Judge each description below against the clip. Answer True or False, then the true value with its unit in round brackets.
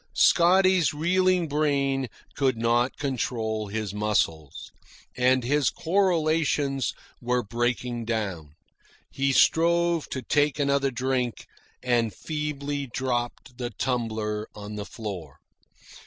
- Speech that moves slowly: True (105 wpm)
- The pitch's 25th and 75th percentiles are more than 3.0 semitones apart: True (4.7 semitones)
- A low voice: True (130 Hz)